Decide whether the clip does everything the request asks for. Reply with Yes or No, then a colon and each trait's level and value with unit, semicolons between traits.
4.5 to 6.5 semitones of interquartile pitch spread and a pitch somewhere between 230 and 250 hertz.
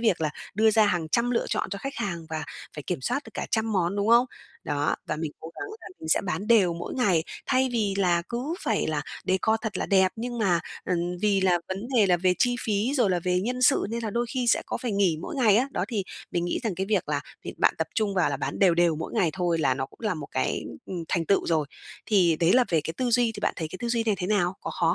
No: average, 5.1 semitones; high, 195 Hz